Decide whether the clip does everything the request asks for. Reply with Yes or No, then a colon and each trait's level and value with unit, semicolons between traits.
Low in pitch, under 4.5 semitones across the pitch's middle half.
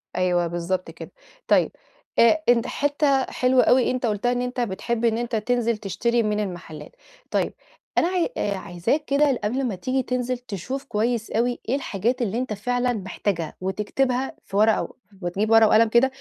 No: high, 235 Hz; average, 3.7 semitones